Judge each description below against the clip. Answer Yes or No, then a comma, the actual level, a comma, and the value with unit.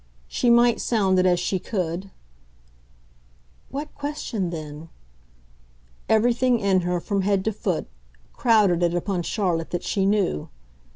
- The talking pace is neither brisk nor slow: No, slow, 130 wpm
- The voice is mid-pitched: No, high, 195 Hz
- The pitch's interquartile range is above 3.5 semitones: Yes, average, 4.0 semitones